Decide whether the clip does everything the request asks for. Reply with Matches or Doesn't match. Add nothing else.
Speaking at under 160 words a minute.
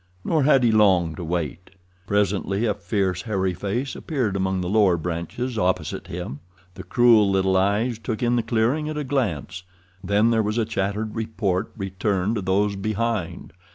Doesn't match